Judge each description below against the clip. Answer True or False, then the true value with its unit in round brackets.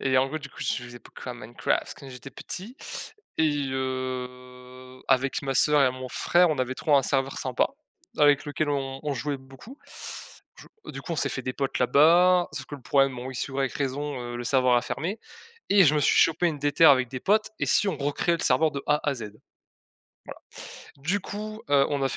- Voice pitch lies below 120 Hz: False (135 Hz)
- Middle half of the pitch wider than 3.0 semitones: False (2.7 semitones)